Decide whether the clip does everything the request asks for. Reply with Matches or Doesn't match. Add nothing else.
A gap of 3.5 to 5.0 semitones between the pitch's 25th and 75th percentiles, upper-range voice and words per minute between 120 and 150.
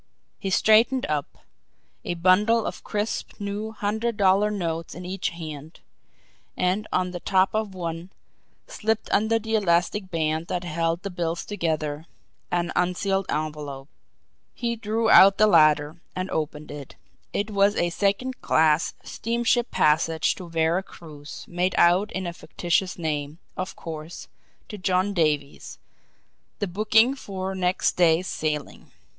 Doesn't match